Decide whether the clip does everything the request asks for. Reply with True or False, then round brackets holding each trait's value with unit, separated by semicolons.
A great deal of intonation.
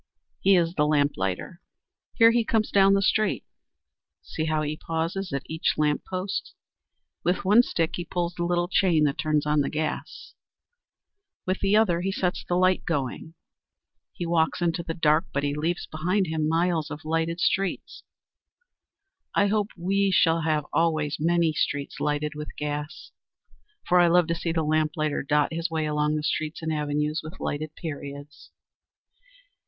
False (2.8 semitones)